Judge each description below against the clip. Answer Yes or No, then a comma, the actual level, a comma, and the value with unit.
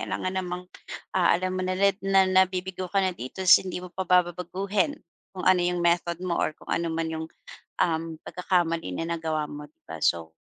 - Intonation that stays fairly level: Yes, narrow, 2.2 semitones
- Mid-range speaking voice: Yes, medium, 180 Hz